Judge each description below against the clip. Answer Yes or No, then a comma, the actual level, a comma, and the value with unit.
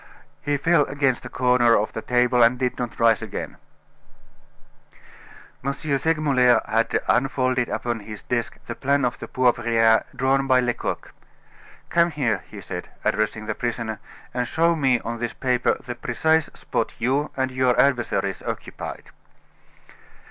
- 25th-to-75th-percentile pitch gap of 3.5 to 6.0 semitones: No, average, 2.7 semitones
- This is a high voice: No, low, 125 Hz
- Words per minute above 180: No, average, 145 wpm